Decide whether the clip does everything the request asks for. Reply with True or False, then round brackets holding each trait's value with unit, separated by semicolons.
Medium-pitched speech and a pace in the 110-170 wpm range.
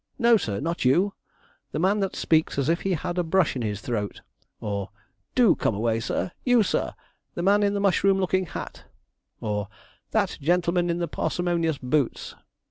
False (170 Hz; 180 wpm)